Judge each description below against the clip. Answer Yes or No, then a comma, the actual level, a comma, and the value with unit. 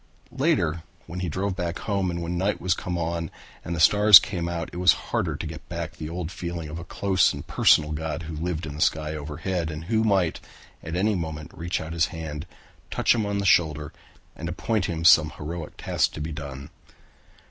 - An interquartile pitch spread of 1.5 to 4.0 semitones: Yes, narrow, 2.6 semitones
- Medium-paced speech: No, fast, 215 wpm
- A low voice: Yes, very low, 85 Hz